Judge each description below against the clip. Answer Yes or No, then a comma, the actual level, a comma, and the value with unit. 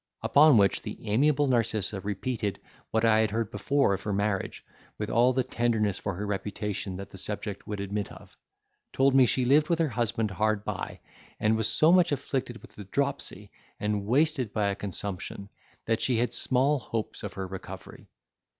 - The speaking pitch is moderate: No, low, 110 Hz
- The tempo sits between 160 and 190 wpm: Yes, average, 185 wpm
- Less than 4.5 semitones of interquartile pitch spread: Yes, average, 4.1 semitones